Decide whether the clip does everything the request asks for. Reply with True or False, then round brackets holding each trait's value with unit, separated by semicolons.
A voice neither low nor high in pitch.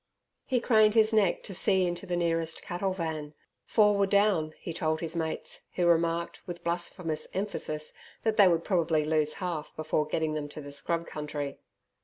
True (170 Hz)